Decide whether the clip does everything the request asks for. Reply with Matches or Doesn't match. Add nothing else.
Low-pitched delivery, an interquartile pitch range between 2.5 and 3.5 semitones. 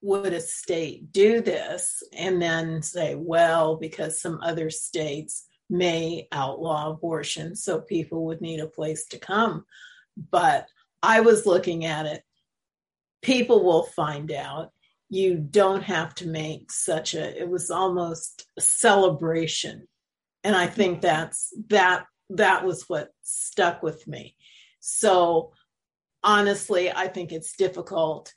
Doesn't match